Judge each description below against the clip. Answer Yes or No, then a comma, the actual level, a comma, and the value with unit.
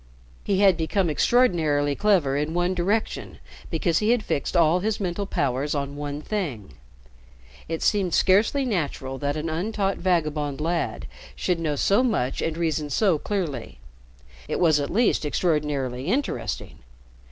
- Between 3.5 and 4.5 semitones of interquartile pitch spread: No, average, 5.1 semitones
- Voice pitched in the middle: Yes, medium, 165 Hz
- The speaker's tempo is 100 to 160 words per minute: Yes, average, 145 wpm